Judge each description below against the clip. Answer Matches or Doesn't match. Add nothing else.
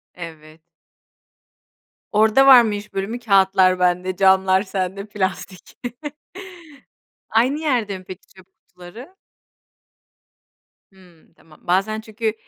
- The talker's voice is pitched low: Doesn't match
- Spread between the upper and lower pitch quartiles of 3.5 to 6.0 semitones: Doesn't match